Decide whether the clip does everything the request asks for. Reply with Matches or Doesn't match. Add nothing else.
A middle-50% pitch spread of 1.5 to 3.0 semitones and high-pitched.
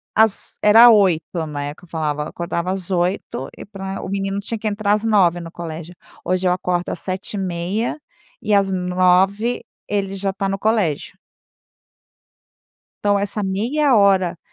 Matches